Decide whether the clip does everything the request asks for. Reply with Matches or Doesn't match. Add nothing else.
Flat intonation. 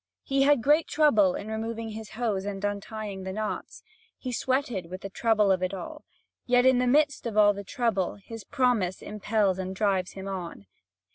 Doesn't match